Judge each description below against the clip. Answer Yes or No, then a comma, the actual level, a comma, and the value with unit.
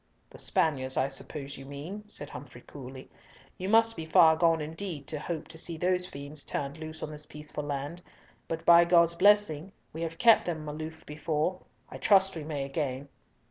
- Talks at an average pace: Yes, average, 185 wpm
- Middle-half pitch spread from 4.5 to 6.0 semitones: No, average, 2.9 semitones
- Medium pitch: Yes, medium, 155 Hz